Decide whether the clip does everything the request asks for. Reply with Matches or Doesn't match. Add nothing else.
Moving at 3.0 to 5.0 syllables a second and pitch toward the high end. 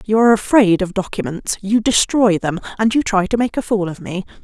Doesn't match